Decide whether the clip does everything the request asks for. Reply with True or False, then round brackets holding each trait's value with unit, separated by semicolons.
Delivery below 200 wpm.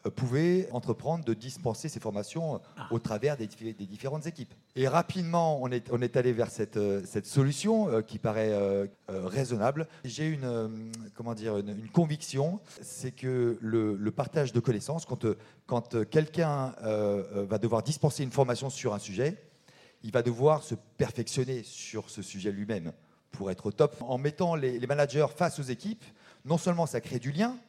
True (150 wpm)